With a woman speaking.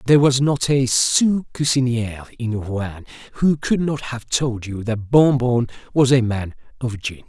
No: male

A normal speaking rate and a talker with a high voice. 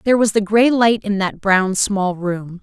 No: fast, 230 wpm; high, 205 Hz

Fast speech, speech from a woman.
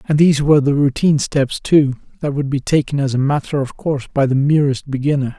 No: fast, 225 wpm; male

